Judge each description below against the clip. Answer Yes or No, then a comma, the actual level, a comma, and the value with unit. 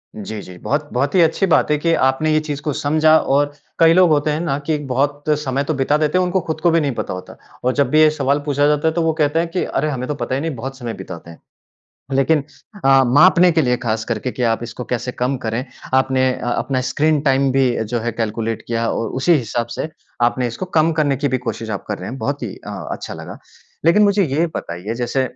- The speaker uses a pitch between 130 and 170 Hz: Yes, medium, 140 Hz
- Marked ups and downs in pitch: No, average, 4.1 semitones